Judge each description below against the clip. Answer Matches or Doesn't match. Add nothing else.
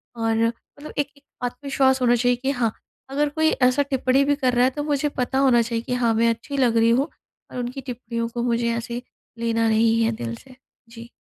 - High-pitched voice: Matches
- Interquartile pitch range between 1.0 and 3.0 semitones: Matches